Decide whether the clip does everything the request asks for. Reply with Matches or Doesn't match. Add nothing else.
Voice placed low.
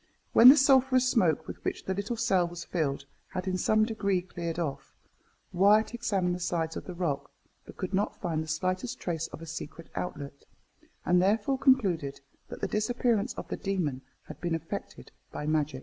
Doesn't match